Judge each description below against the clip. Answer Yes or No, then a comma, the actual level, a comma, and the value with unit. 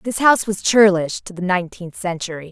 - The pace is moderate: Yes, average, 190 wpm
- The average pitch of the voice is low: No, high, 190 Hz